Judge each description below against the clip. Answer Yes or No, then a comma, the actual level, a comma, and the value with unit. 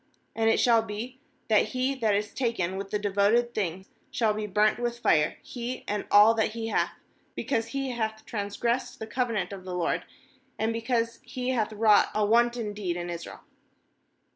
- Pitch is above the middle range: Yes, high, 220 Hz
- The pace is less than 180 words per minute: No, average, 185 wpm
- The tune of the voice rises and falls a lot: No, narrow, 2.6 semitones